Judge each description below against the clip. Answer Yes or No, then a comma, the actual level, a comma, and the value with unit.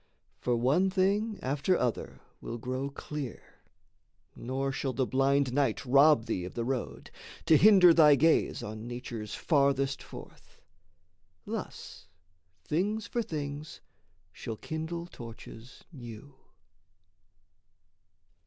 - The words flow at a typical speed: No, slow, 110 wpm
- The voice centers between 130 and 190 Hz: Yes, medium, 140 Hz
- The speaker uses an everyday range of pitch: Yes, average, 4.6 semitones